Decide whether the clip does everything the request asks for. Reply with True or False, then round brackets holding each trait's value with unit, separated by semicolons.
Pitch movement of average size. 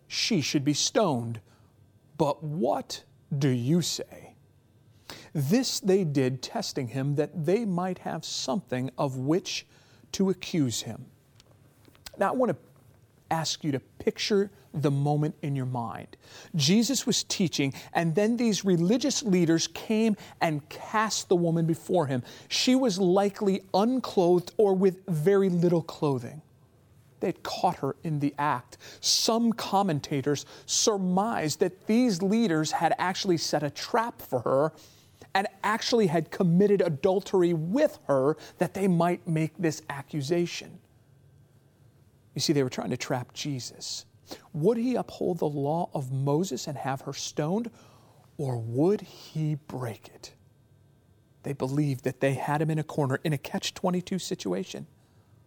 False (6.2 semitones)